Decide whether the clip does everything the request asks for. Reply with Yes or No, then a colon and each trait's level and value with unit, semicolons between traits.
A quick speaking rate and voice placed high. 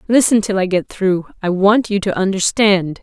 No: average, 180 wpm; high, 195 Hz